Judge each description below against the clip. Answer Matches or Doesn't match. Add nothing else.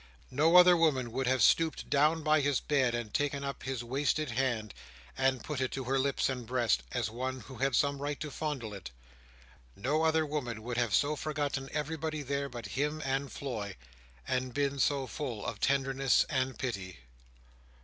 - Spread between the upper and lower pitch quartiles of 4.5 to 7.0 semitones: Doesn't match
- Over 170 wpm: Matches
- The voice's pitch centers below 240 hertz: Matches